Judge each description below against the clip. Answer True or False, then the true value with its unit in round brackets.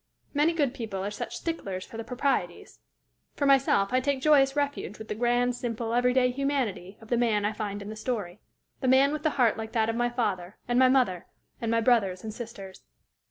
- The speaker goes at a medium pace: False (215 wpm)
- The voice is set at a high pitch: True (240 Hz)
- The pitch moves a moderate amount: True (3.8 semitones)